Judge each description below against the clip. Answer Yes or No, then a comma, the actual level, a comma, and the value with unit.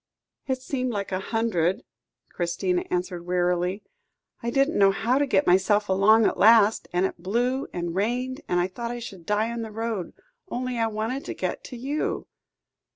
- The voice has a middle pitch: No, high, 215 Hz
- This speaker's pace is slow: No, average, 180 wpm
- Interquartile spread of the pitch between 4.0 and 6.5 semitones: Yes, average, 4.5 semitones